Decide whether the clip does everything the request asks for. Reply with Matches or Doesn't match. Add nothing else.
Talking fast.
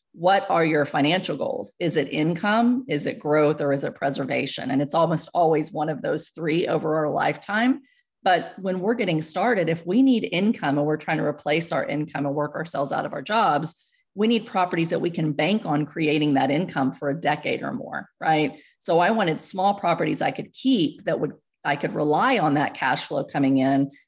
Matches